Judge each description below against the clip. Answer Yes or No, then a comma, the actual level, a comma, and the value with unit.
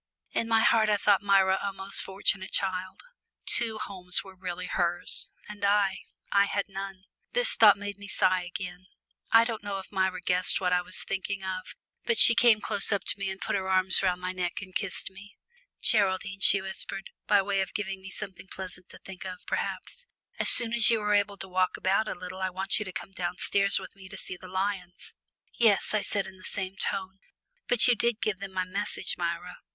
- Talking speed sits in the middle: No, fast, 215 wpm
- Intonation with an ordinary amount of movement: No, narrow, 1.5 semitones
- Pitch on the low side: No, high, 195 Hz